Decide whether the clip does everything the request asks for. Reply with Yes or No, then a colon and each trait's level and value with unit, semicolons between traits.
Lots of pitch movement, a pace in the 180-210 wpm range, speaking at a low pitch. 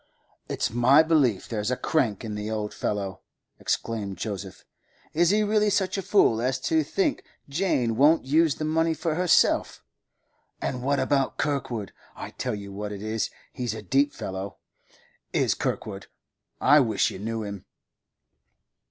No: wide, 6.8 semitones; average, 155 wpm; low, 125 Hz